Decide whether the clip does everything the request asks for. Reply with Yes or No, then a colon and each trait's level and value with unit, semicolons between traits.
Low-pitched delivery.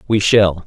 Yes: low, 100 Hz